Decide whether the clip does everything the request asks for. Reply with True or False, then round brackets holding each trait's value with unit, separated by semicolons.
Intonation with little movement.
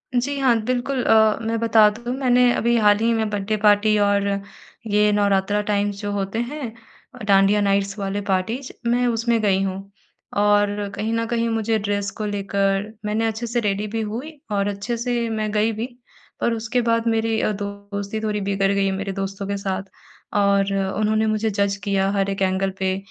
True (2.2 semitones)